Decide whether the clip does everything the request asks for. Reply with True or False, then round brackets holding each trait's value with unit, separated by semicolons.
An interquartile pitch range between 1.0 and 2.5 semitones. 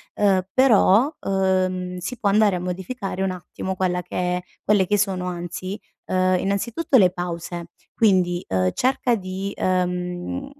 True (2.0 semitones)